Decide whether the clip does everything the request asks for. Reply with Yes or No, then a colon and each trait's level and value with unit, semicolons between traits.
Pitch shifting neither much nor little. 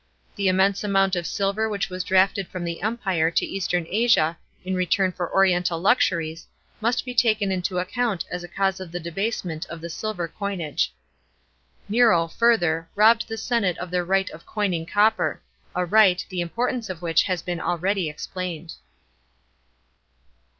Yes: average, 3.2 semitones